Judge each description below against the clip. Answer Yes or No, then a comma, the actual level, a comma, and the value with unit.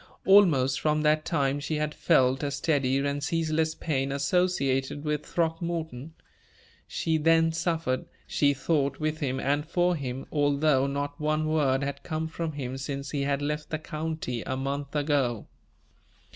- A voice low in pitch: No, medium, 145 Hz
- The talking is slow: No, average, 155 wpm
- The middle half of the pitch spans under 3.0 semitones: Yes, narrow, 2.4 semitones